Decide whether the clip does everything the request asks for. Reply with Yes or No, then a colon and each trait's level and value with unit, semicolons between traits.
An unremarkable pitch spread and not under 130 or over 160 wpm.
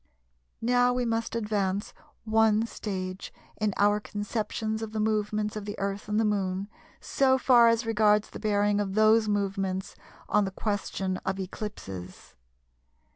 No: narrow, 1.8 semitones; average, 150 wpm